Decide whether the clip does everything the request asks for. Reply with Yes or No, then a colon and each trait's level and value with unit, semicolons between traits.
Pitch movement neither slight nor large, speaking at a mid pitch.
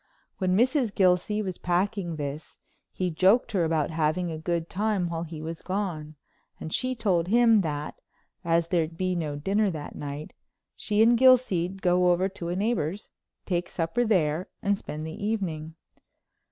Yes: average, 3.9 semitones; medium, 180 Hz